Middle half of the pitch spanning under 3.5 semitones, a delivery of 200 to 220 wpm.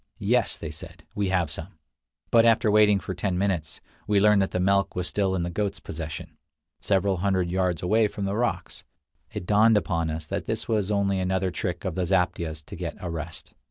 Yes: average, 2.8 semitones; fast, 205 wpm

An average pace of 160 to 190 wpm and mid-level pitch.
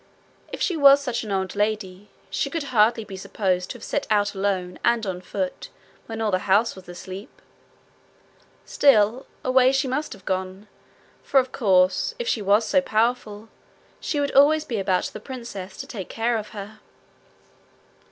No: average, 170 wpm; high, 215 Hz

